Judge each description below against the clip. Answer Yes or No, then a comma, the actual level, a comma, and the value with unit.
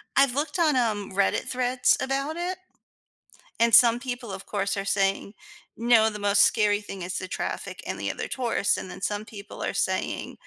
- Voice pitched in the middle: No, high, 220 Hz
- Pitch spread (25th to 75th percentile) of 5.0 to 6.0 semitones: No, average, 4.1 semitones